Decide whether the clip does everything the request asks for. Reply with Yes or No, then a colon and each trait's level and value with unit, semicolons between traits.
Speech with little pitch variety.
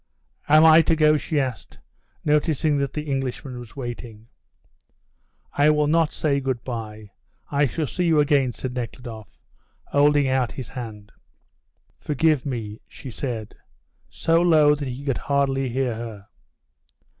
No: average, 3.7 semitones